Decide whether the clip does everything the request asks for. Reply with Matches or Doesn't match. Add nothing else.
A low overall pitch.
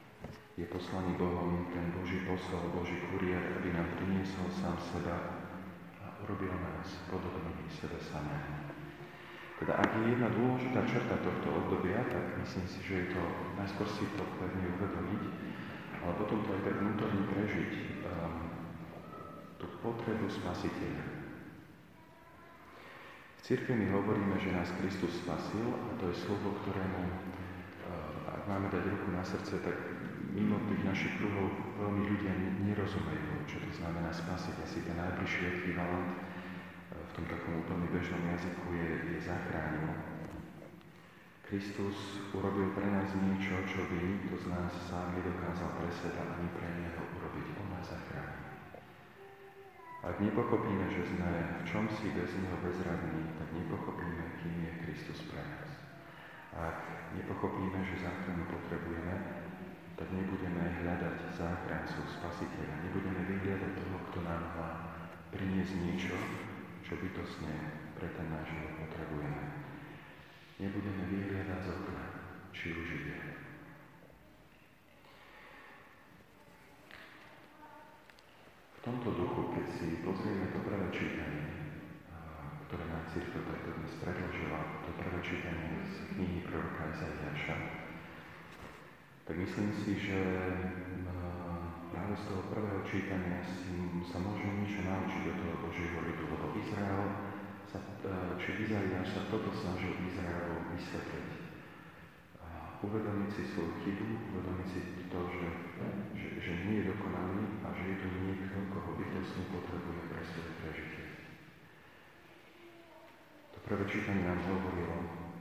Matches